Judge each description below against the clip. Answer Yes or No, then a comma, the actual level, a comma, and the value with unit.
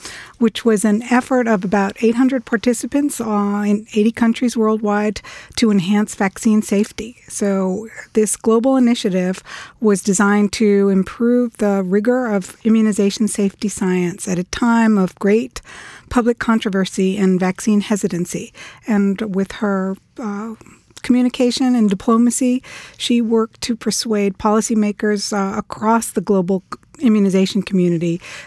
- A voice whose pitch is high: Yes, high, 215 Hz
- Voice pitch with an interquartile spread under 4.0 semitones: Yes, narrow, 2.6 semitones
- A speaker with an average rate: No, slow, 125 wpm